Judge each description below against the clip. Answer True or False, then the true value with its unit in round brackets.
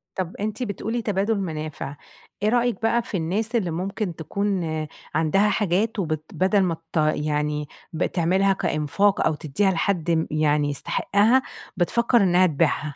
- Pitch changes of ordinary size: True (4.8 semitones)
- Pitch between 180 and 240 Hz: True (185 Hz)